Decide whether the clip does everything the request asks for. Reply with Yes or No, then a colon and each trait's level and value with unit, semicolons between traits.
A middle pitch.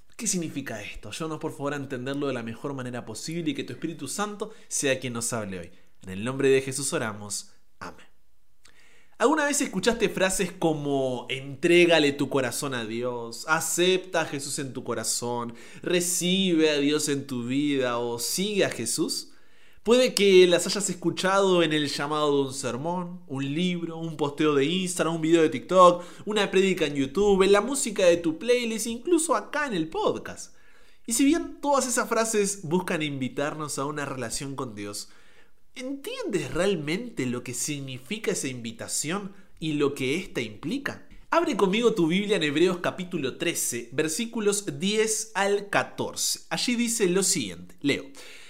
Yes: medium, 160 Hz